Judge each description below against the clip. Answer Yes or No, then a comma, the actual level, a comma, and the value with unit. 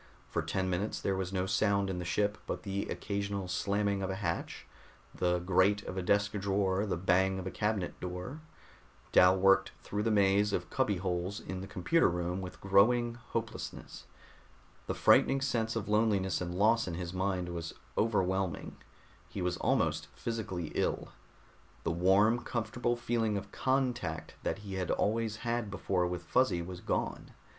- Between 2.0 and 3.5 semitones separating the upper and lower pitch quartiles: Yes, average, 2.8 semitones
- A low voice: Yes, very low, 95 Hz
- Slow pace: No, average, 165 wpm